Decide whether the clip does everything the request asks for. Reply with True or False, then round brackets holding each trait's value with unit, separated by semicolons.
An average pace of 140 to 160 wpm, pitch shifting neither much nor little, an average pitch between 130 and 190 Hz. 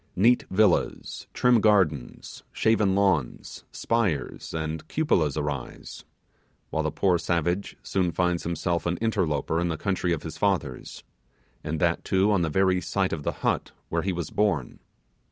False (155 wpm; 3.6 semitones; 90 Hz)